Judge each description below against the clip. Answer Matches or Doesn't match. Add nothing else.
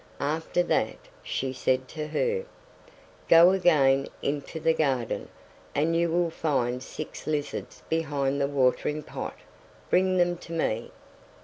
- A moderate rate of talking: Doesn't match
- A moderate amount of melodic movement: Matches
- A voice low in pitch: Doesn't match